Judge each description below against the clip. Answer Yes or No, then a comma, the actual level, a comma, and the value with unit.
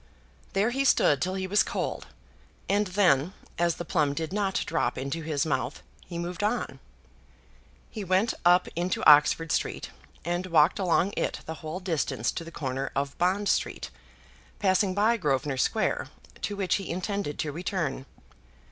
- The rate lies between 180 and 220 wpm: No, average, 160 wpm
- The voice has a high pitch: No, medium, 175 Hz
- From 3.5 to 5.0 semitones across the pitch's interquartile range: Yes, average, 4.3 semitones